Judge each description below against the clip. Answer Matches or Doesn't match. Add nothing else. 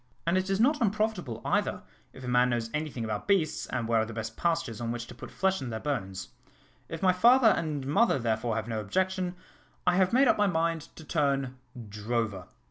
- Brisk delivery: Matches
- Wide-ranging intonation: Matches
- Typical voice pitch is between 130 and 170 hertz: Matches